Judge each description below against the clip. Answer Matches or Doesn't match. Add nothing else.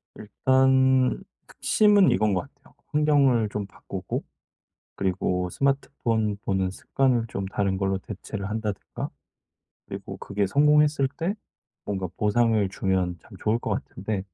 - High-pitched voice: Doesn't match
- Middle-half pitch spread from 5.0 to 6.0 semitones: Matches